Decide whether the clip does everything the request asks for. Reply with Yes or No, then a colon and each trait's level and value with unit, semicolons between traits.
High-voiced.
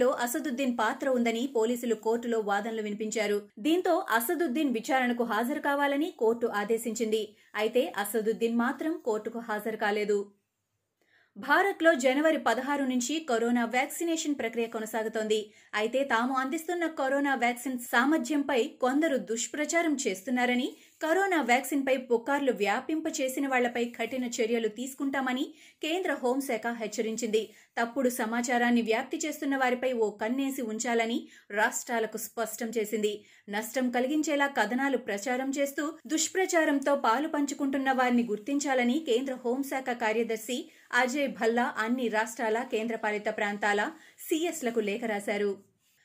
Yes: high, 245 Hz